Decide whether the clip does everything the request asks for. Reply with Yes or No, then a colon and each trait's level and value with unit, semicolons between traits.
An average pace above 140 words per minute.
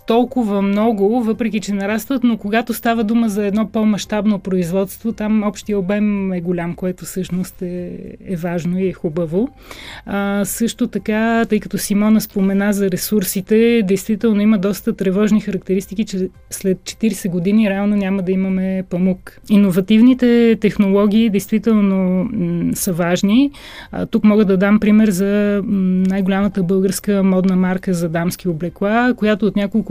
Yes: average, 150 wpm